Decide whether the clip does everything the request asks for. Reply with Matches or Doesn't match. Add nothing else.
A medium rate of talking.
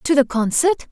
Matches